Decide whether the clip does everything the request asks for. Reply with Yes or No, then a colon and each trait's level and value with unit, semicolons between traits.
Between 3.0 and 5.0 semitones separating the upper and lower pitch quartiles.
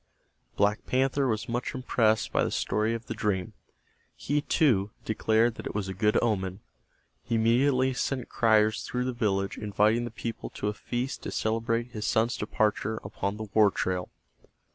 No: narrow, 2.4 semitones